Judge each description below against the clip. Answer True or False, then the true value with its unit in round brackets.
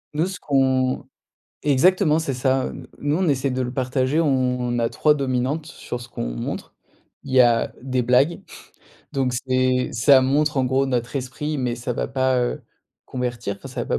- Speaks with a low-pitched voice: True (130 Hz)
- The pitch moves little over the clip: True (2.1 semitones)